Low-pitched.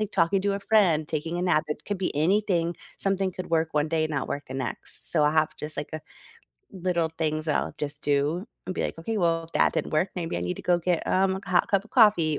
No: medium, 165 Hz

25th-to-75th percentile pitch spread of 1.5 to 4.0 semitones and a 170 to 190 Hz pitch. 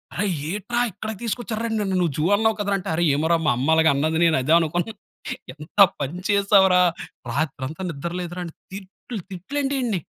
No: average, 4.7 semitones; medium, 185 Hz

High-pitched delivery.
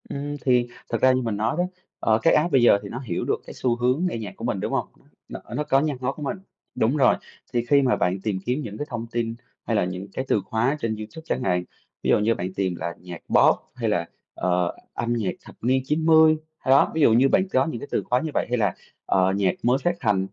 No: low, 120 Hz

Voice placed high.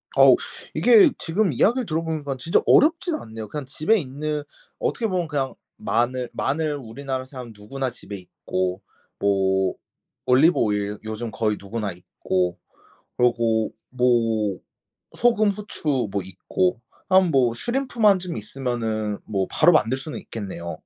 No: low, 130 Hz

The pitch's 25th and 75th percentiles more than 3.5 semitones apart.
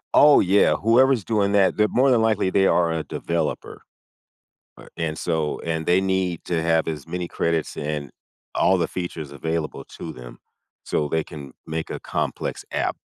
Yes: average, 3.9 semitones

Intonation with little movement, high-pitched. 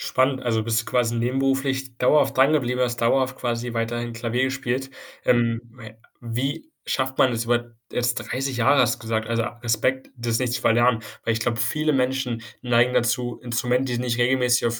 No: narrow, 2.0 semitones; low, 120 Hz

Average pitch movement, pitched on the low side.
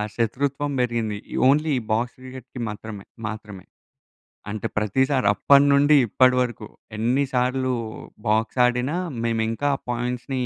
Yes: average, 3.1 semitones; low, 125 Hz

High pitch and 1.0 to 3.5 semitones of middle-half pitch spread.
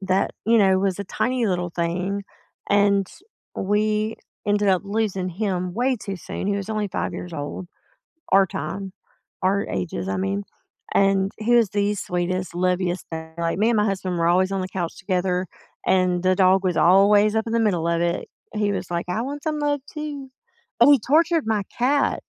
Yes: high, 195 Hz; average, 3.0 semitones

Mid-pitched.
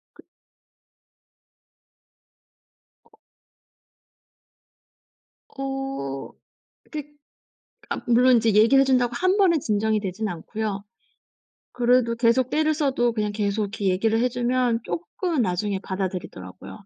No: high, 230 Hz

